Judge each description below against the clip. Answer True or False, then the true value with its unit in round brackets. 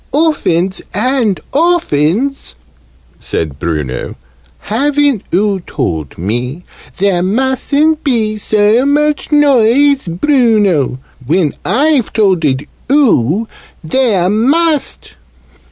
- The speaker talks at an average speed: False (85 wpm)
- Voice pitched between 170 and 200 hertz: False (215 Hz)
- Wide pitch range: True (8.6 semitones)